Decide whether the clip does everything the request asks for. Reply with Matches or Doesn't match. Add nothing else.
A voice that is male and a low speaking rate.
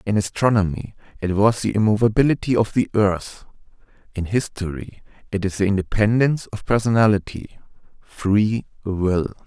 Matches